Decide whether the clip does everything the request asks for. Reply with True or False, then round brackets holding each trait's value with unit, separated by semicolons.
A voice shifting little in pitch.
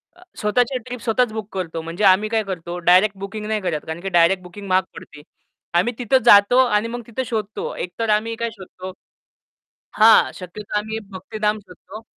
False (3.3 semitones)